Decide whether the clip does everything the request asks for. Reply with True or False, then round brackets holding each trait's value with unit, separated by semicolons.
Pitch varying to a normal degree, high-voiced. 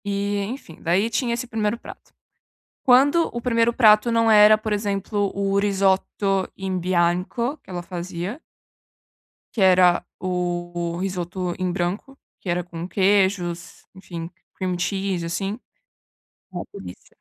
True (3.2 semitones; 195 Hz)